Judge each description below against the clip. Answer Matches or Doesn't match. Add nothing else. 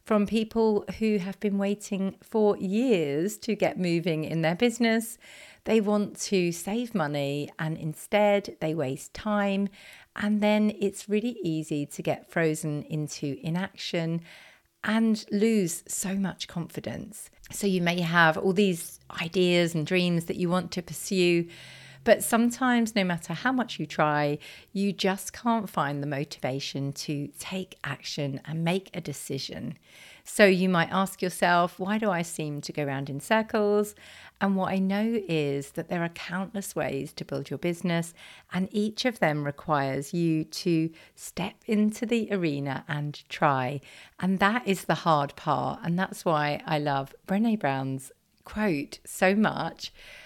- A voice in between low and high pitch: Matches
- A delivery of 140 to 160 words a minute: Matches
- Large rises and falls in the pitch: Doesn't match